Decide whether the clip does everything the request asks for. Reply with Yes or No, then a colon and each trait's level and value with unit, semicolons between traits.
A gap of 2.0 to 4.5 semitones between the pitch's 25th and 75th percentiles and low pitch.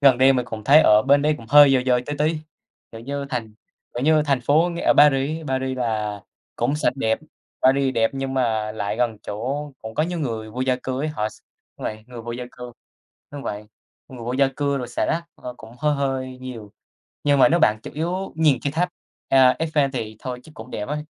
Yes: average, 3.8 semitones; low, 130 Hz